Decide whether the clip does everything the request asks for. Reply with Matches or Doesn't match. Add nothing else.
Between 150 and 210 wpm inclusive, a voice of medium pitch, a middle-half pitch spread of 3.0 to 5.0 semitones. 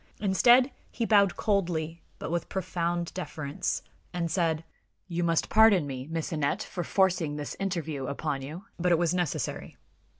Matches